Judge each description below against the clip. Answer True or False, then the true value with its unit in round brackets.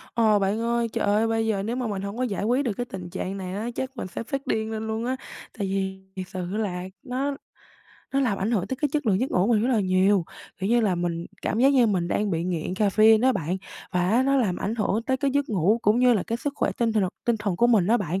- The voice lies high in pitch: True (215 Hz)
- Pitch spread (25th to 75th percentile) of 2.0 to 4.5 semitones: True (3.8 semitones)